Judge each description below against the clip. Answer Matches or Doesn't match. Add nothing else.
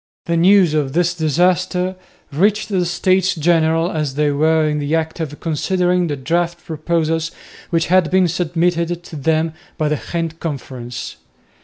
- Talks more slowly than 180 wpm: Matches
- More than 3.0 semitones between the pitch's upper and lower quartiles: Doesn't match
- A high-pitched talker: Doesn't match